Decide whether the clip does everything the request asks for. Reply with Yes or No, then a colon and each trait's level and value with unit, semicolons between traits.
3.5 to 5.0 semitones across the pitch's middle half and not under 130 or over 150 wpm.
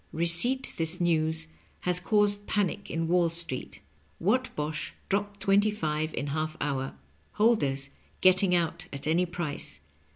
Yes: average, 4.4 semitones; slow, 135 wpm